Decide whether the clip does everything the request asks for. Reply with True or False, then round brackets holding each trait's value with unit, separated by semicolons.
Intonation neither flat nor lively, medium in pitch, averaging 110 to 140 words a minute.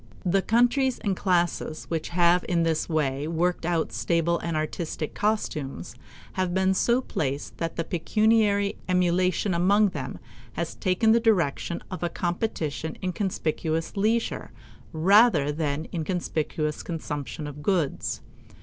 True (3.8 semitones; 175 Hz; 135 wpm)